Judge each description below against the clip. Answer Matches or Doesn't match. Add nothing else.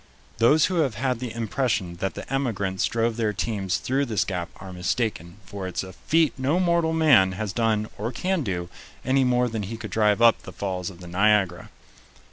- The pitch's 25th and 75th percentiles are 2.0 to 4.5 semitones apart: Doesn't match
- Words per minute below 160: Doesn't match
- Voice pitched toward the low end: Matches